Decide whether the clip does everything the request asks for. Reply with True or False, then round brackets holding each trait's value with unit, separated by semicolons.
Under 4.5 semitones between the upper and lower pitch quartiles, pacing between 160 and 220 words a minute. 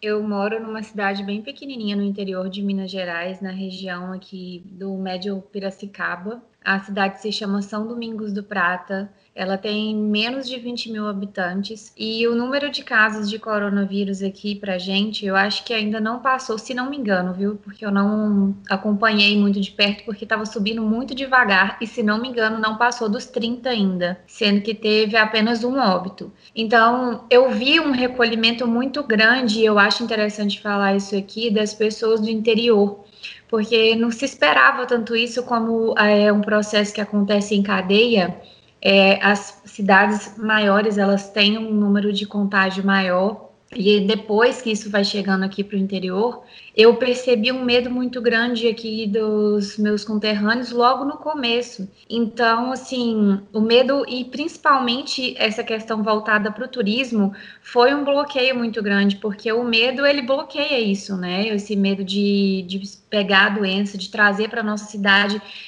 True (2.7 semitones; 165 wpm)